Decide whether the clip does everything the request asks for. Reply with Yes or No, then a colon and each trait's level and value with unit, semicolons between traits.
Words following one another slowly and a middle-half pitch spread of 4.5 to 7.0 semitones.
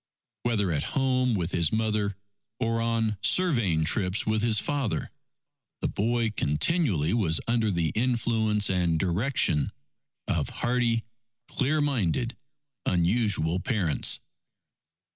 Yes: slow, 110 wpm; average, 5.0 semitones